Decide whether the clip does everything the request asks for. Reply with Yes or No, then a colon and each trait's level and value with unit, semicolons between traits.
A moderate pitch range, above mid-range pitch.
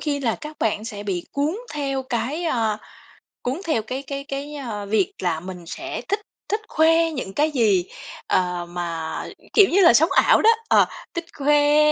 No: wide, 6.7 semitones; very high, 265 Hz